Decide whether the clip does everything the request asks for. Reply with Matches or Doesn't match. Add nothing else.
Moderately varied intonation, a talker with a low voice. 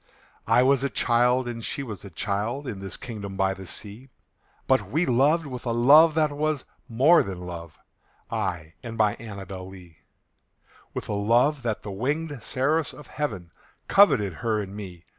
Doesn't match